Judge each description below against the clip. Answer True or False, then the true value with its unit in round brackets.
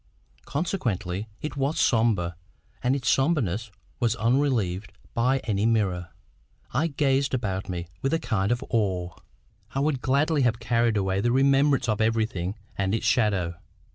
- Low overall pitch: True (115 Hz)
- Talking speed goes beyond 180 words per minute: False (145 wpm)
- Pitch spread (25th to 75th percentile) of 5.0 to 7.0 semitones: True (5.5 semitones)